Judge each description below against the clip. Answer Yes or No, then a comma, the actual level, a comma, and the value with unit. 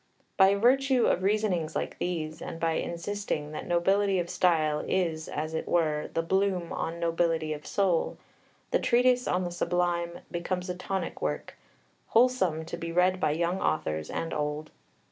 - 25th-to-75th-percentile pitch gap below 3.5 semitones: Yes, average, 3.1 semitones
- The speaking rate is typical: Yes, average, 165 wpm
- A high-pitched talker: No, medium, 175 Hz